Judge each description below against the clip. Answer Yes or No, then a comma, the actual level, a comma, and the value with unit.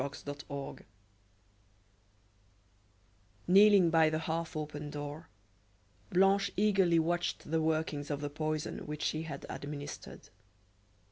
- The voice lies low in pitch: No, medium, 155 Hz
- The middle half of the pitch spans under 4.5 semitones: Yes, narrow, 2.6 semitones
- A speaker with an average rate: No, slow, 110 wpm